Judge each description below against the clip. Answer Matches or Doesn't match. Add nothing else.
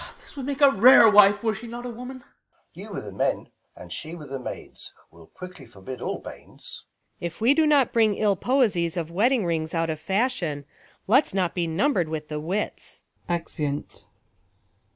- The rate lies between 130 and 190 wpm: Doesn't match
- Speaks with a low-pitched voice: Doesn't match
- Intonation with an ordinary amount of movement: Doesn't match